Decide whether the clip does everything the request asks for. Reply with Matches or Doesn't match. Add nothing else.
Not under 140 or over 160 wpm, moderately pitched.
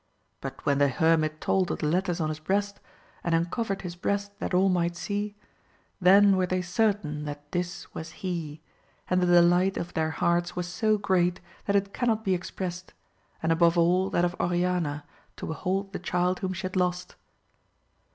Doesn't match